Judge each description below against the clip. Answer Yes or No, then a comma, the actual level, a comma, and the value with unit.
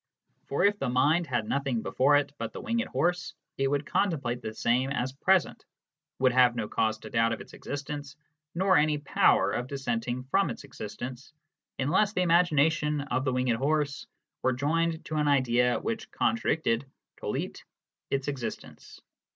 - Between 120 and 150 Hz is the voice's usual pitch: Yes, medium, 140 Hz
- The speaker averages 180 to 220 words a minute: No, average, 165 wpm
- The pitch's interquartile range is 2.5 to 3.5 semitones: No, average, 4.1 semitones